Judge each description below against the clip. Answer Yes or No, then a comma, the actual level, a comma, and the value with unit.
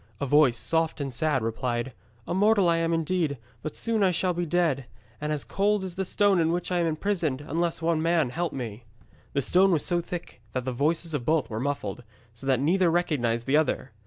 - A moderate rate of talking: No, fast, 215 wpm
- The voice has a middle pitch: Yes, medium, 160 Hz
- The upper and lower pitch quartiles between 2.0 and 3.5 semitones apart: No, average, 4.6 semitones